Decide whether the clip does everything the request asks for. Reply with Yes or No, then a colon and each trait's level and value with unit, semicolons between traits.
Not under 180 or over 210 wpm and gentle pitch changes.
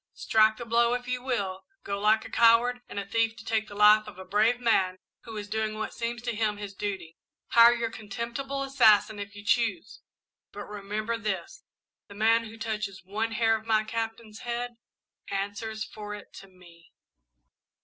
Yes: average, 185 wpm; narrow, 2.2 semitones